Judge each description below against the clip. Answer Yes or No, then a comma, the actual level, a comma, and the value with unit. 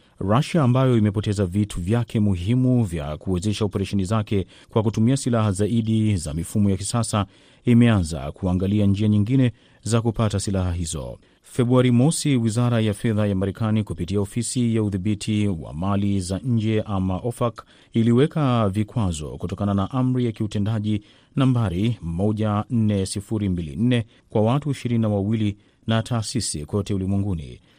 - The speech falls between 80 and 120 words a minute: No, average, 130 wpm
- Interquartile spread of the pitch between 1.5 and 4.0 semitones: Yes, average, 3.1 semitones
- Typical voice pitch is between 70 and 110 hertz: Yes, low, 105 Hz